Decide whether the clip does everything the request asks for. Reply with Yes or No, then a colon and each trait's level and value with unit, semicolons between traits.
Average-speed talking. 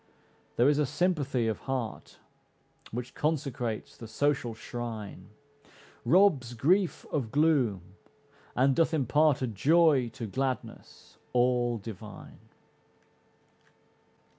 No: slow, 100 wpm